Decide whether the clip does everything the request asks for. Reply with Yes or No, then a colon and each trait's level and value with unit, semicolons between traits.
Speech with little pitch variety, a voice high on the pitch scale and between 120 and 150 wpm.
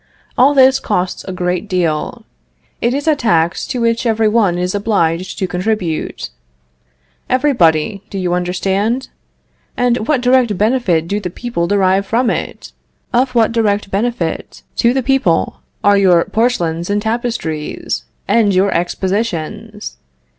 No: average, 4.9 semitones; high, 205 Hz; average, 140 wpm